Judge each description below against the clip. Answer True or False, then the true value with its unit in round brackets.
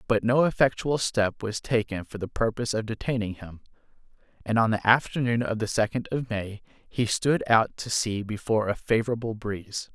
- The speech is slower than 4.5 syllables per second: False (5.2 syllables/s)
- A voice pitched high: False (110 Hz)